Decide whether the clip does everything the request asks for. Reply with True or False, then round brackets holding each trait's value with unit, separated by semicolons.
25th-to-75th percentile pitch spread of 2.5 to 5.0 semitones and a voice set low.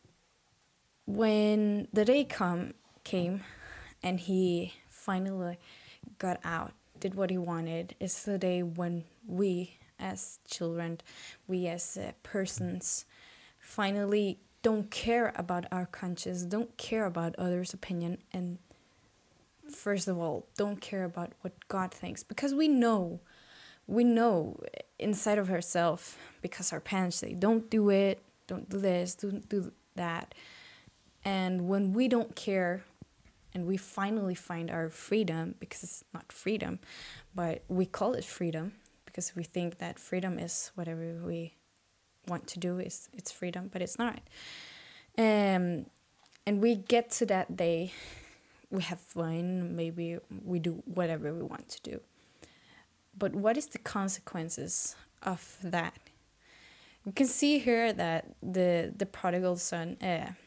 False (3.0 semitones; 185 Hz)